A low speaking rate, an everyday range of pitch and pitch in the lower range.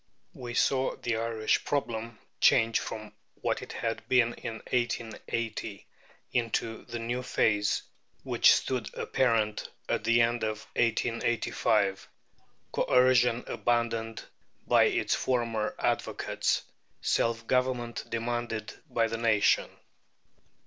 No: slow, 105 wpm; narrow, 1.2 semitones; low, 115 Hz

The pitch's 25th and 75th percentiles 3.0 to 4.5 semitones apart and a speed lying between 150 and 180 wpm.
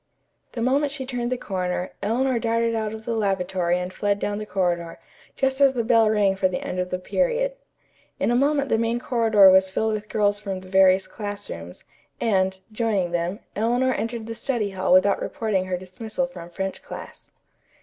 No: average, 3.9 semitones; average, 190 wpm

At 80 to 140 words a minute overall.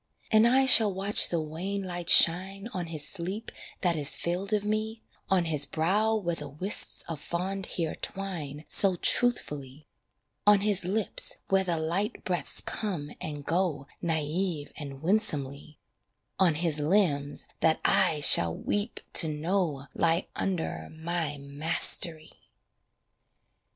Yes: slow, 135 wpm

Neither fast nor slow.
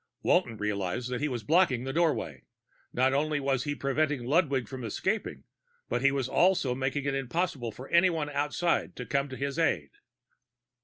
Yes: average, 170 wpm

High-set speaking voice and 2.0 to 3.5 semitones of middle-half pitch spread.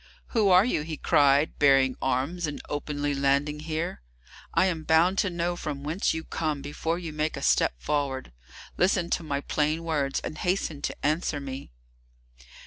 No: medium, 150 Hz; average, 2.9 semitones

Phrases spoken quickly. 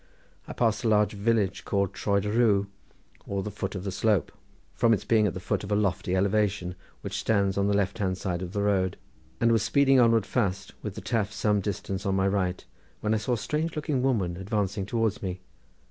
Yes: fast, 225 wpm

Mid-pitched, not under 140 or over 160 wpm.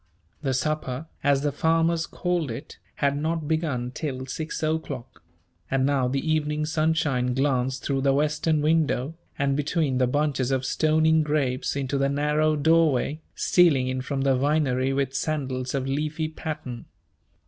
Yes: medium, 145 Hz; average, 150 wpm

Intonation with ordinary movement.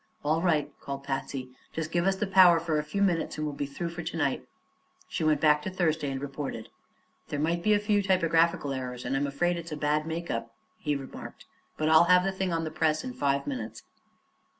Yes: average, 3.5 semitones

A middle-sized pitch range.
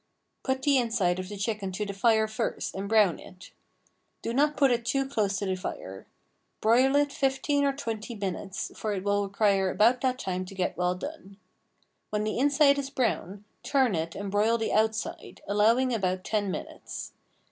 Yes: average, 4.8 semitones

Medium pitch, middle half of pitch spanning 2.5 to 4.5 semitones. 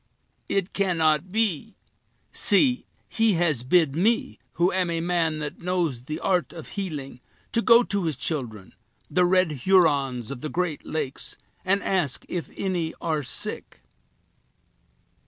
Yes: medium, 170 Hz; average, 4.1 semitones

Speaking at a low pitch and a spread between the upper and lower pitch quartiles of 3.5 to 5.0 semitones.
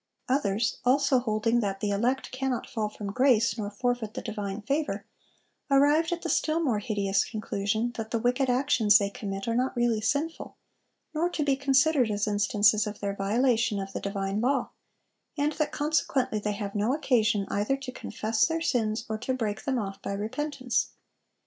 No: high, 230 Hz; average, 4.5 semitones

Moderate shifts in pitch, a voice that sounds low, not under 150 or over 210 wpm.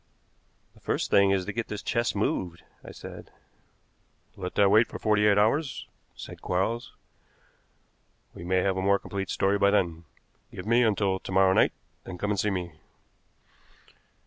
No: narrow, 2.0 semitones; low, 100 Hz; average, 170 wpm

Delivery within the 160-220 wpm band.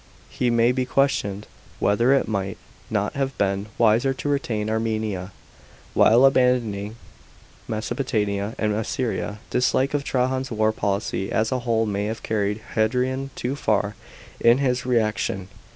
No: average, 140 wpm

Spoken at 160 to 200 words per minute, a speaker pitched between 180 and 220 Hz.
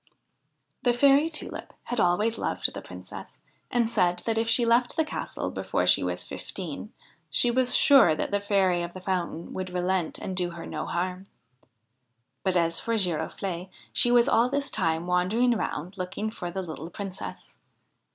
Yes: average, 170 wpm; high, 190 Hz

